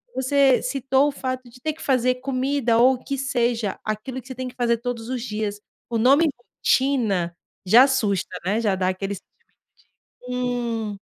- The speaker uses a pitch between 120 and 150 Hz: No, high, 245 Hz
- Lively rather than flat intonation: No, average, 3.2 semitones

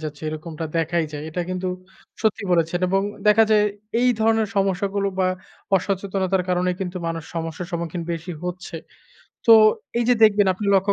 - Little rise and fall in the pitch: No, average, 3.2 semitones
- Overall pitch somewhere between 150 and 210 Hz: Yes, medium, 185 Hz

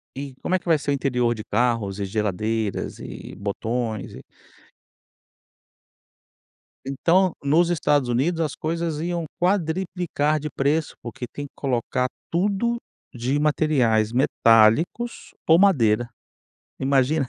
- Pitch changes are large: Yes, wide, 5.8 semitones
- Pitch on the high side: No, medium, 140 Hz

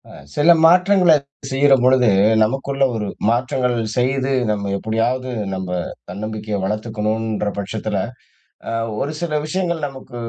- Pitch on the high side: No, low, 125 Hz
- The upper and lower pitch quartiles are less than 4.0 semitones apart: No, average, 4.4 semitones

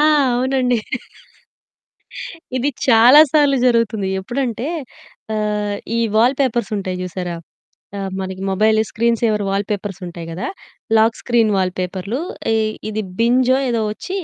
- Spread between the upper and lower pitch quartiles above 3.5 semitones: Yes, average, 4.0 semitones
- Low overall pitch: No, high, 220 Hz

